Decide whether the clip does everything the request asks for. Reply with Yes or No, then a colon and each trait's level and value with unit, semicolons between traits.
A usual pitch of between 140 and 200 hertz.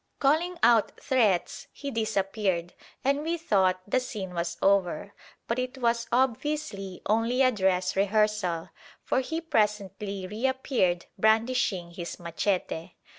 No: high, 210 Hz